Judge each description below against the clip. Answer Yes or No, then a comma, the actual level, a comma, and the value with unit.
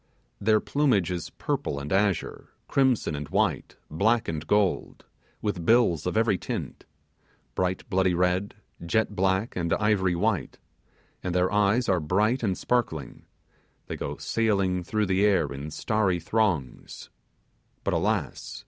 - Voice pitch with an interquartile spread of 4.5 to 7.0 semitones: No, average, 3.5 semitones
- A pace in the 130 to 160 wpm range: Yes, average, 140 wpm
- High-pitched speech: No, very low, 95 Hz